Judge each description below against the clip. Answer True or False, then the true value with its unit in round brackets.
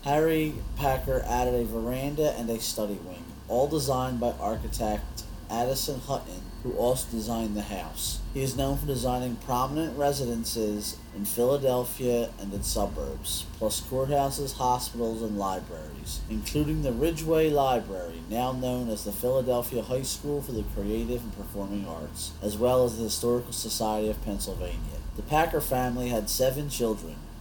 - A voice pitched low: True (120 Hz)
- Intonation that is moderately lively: True (3.9 semitones)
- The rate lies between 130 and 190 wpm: True (150 wpm)